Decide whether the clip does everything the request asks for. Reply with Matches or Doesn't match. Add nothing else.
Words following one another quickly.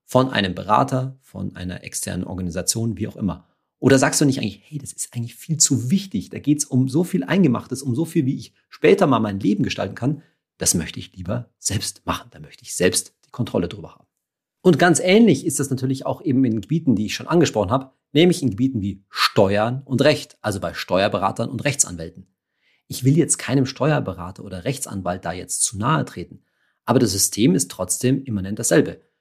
Matches